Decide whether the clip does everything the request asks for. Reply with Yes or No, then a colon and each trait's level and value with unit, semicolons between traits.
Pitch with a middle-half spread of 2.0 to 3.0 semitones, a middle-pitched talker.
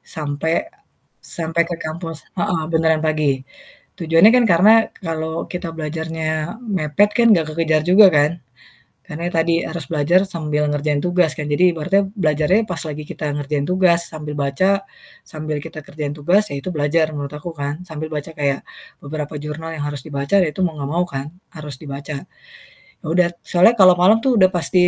Yes: narrow, 2.6 semitones; medium, 160 Hz